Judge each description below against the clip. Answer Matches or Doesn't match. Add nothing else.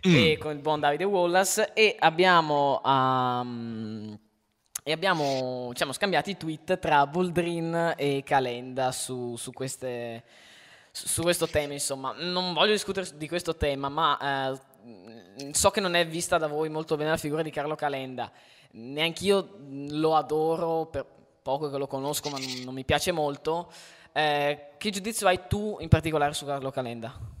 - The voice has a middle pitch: Matches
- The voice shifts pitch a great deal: Doesn't match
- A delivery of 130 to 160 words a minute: Matches